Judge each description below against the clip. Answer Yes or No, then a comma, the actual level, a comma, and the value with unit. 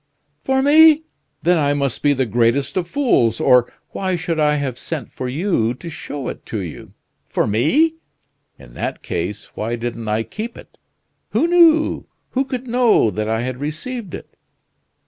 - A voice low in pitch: No, medium, 145 Hz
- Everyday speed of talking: Yes, average, 165 wpm